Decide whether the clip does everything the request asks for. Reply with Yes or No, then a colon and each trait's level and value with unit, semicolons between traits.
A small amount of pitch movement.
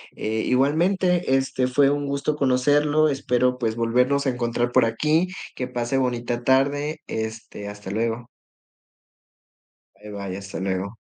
No: average, 3.7 semitones